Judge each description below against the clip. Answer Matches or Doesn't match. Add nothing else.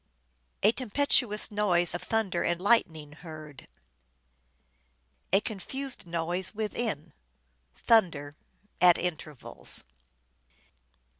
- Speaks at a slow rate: Matches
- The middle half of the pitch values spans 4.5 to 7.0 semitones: Matches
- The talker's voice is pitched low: Doesn't match